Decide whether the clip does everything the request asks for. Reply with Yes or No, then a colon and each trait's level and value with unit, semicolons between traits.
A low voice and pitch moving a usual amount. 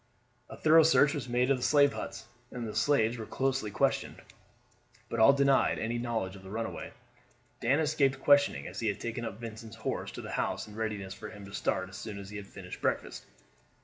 Yes: low, 115 Hz; average, 4.3 semitones